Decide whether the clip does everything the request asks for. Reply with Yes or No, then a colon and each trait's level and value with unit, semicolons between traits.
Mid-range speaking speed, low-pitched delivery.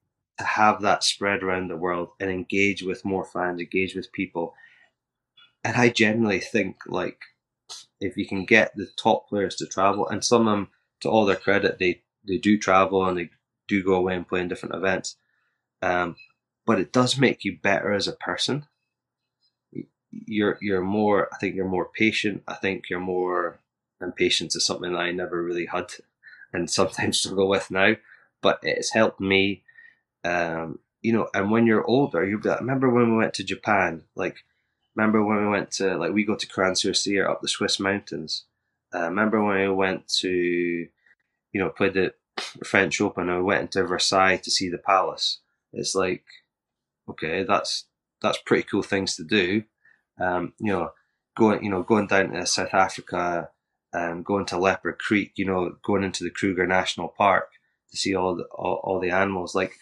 Yes: average, 185 wpm; very low, 95 Hz